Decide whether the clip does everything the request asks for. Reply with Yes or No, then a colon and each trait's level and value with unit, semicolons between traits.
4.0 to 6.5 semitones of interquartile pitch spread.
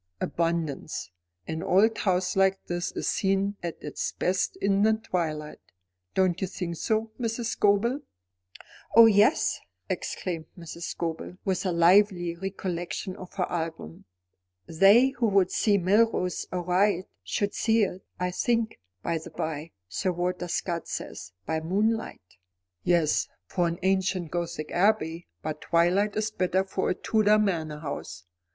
No: average, 3.2 semitones